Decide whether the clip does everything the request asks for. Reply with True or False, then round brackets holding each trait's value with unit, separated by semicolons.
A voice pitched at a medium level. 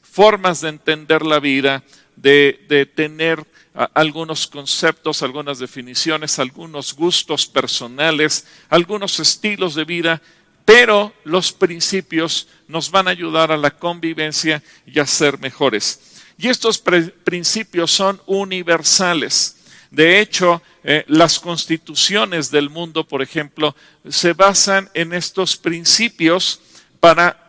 True (165 Hz)